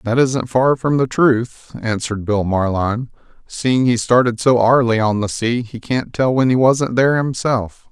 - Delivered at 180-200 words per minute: Yes, average, 190 wpm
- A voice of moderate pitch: No, low, 120 Hz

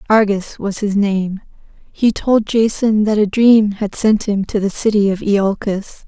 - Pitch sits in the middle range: No, high, 205 Hz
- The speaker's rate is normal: Yes, average, 180 wpm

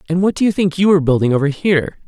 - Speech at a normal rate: No, fast, 290 wpm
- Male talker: Yes, male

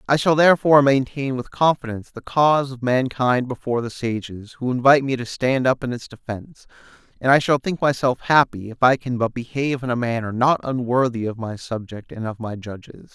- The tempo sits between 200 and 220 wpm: Yes, fast, 205 wpm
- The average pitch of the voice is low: Yes, low, 125 Hz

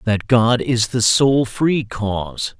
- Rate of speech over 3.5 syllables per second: No, 3.2 syllables/s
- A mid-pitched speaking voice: No, low, 115 Hz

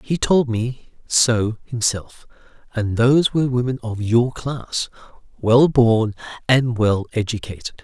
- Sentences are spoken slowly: Yes, slow, 130 wpm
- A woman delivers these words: No, male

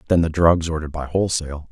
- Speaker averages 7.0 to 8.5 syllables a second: Yes, 7.3 syllables/s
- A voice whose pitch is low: Yes, very low, 80 Hz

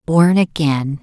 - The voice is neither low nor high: Yes, medium, 155 Hz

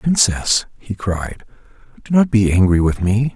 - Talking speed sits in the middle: Yes, average, 160 wpm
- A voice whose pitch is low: Yes, low, 110 Hz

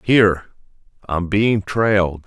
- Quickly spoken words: No, slow, 105 wpm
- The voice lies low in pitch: Yes, very low, 95 Hz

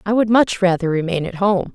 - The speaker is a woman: Yes, female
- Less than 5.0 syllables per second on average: No, 5.5 syllables/s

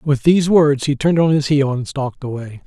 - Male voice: Yes, male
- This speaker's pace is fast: Yes, fast, 245 wpm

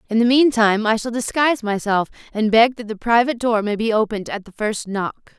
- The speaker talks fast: Yes, fast, 235 wpm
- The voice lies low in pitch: No, high, 225 Hz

